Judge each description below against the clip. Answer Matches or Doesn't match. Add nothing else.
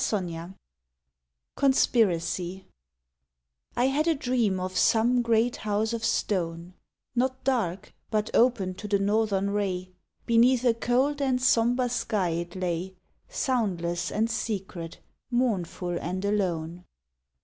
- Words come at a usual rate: Doesn't match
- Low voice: Doesn't match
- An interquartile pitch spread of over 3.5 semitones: Matches